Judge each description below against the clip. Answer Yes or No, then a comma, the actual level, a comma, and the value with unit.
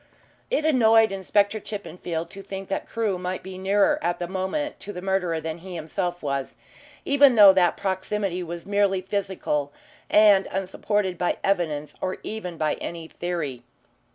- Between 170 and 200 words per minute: No, average, 155 wpm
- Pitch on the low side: No, high, 190 Hz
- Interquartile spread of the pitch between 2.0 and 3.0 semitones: Yes, average, 2.7 semitones